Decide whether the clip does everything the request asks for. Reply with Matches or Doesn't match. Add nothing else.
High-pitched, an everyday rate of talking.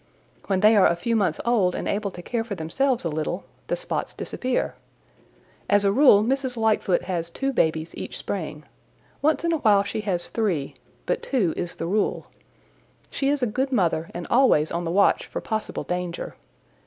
Matches